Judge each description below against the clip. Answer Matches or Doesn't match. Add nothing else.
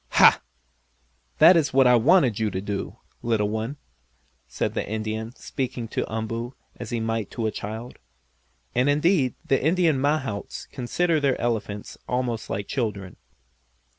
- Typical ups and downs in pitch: Matches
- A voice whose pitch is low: Matches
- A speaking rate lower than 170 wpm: Matches